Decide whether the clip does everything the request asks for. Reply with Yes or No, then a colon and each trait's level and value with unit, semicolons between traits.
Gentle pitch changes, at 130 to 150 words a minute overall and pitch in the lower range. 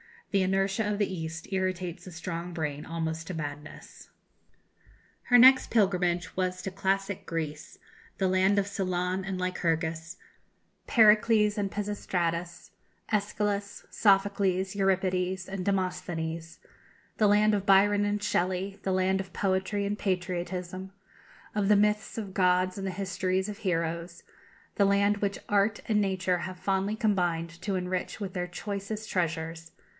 No: narrow, 2.2 semitones; average, 140 wpm; high, 190 Hz